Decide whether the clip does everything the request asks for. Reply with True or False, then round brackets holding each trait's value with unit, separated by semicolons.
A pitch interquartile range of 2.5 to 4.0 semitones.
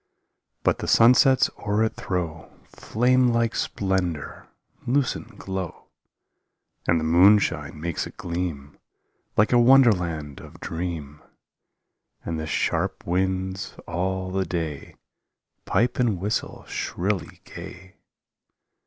False (4.6 semitones)